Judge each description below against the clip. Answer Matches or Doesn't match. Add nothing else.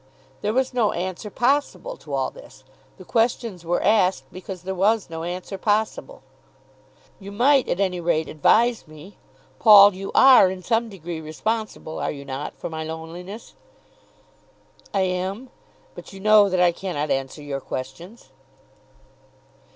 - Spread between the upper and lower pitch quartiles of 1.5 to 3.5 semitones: Doesn't match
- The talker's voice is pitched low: Doesn't match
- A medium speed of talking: Matches